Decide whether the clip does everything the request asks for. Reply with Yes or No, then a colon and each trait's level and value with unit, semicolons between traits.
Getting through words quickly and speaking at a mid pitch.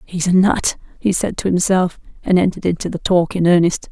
Yes: fast, 215 wpm; medium, 180 Hz